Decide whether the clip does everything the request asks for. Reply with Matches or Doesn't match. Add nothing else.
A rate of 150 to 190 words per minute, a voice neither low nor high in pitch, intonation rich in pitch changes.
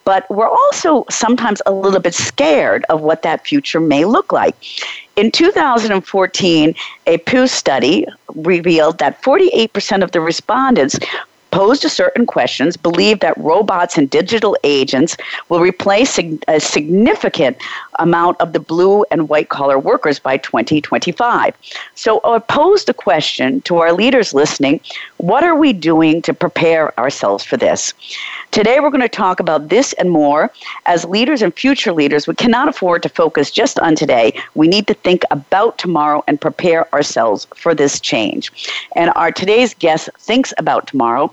Matches